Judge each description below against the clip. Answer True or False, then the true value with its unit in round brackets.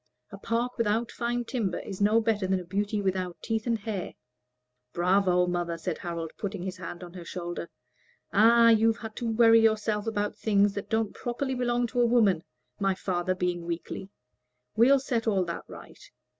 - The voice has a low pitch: False (205 Hz)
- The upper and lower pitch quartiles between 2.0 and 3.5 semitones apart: False (3.9 semitones)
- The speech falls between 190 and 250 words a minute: False (180 wpm)